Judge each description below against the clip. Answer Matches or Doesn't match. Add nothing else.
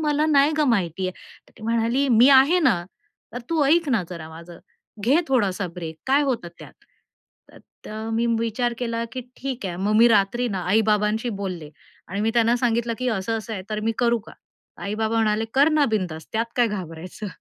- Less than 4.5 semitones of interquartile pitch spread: Matches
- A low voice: Doesn't match